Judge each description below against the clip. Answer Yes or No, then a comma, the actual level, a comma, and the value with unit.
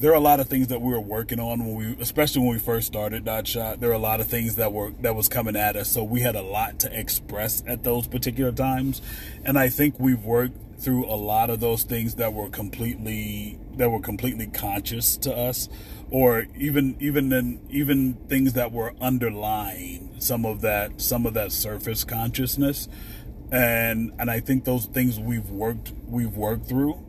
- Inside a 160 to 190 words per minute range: No, fast, 205 wpm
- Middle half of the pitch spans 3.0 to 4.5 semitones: No, narrow, 2.5 semitones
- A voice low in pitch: Yes, low, 115 Hz